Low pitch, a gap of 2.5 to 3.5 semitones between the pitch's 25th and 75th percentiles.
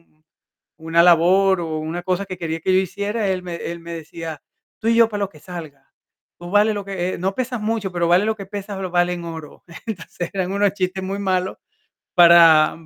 No: medium, 180 Hz; average, 2.8 semitones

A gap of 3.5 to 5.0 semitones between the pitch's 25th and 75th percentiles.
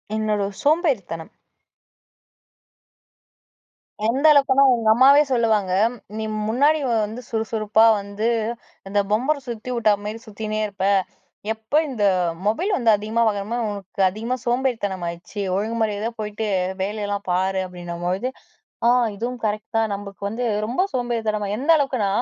No: average, 3.0 semitones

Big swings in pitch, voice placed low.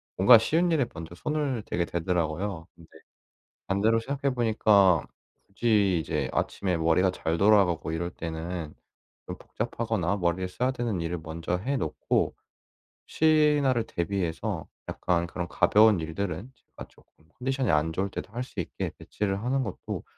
Yes: wide, 5.7 semitones; very low, 95 Hz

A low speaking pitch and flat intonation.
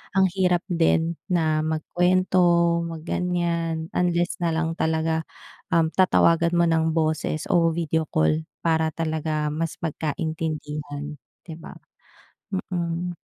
No: medium, 165 Hz; narrow, 1.5 semitones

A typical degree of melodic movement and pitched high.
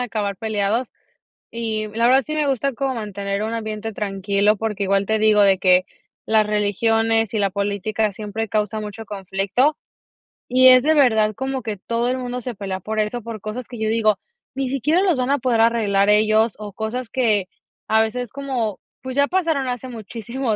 Yes: average, 3.2 semitones; high, 220 Hz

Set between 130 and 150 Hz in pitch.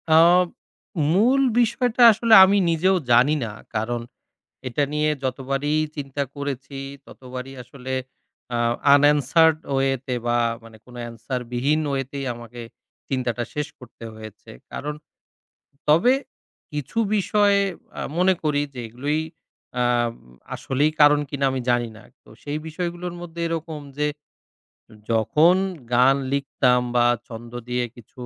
Yes: medium, 140 Hz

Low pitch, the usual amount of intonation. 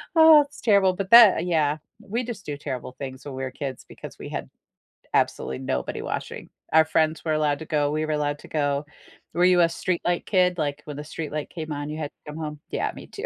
No: medium, 155 Hz; average, 3.7 semitones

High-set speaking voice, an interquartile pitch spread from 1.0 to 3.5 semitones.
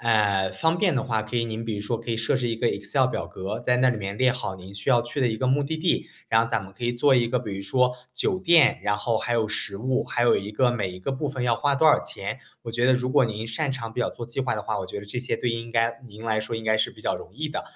No: low, 115 Hz; average, 3.0 semitones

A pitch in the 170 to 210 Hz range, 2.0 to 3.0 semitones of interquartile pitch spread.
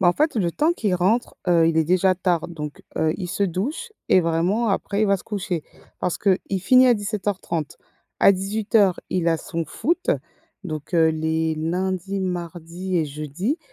No: medium, 185 Hz; average, 3.5 semitones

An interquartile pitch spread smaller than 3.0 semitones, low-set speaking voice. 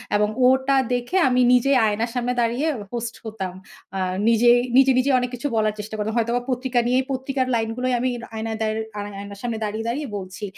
No: narrow, 2.6 semitones; high, 235 Hz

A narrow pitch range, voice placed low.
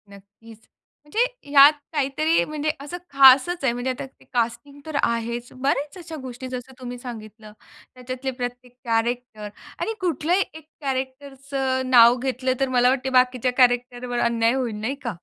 No: narrow, 2.3 semitones; very high, 255 Hz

